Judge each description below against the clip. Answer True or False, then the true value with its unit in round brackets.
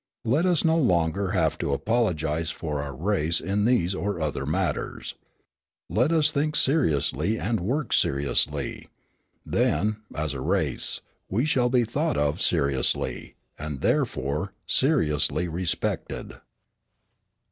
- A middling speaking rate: False (125 wpm)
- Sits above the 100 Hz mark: False (95 Hz)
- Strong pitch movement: True (8.5 semitones)